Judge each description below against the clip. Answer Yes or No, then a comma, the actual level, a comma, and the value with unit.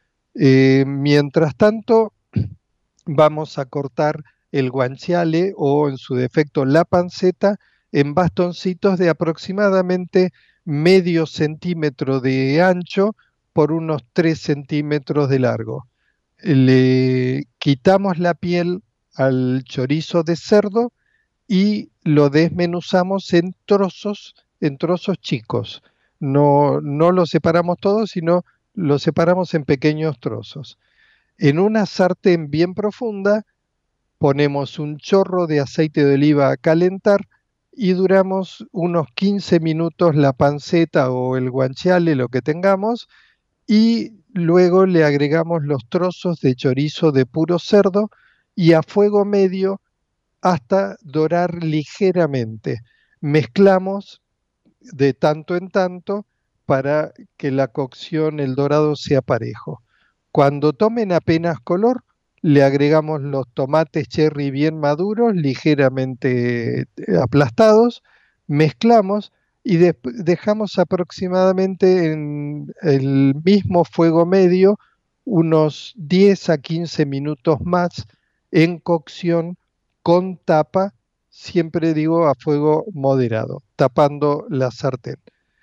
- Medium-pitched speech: Yes, medium, 165 Hz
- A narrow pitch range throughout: No, average, 4.4 semitones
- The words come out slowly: Yes, slow, 105 wpm